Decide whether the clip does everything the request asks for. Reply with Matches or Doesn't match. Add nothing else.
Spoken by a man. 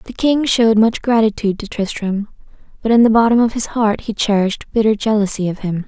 Doesn't match